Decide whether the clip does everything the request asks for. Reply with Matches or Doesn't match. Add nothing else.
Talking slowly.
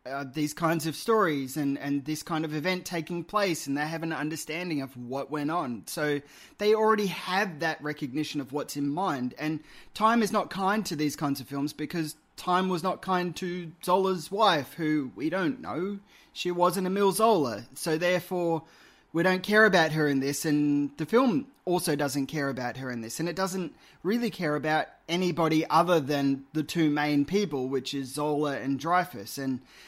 Doesn't match